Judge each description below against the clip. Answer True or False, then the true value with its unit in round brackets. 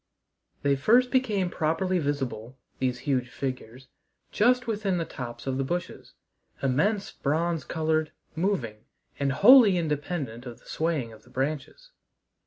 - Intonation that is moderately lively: False (6.2 semitones)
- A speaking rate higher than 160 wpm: False (135 wpm)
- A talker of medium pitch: True (155 Hz)